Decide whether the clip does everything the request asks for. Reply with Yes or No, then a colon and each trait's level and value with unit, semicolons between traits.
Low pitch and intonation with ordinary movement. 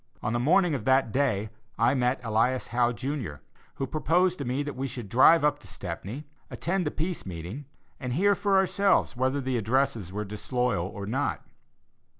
Yes: low, 130 Hz; average, 4.8 semitones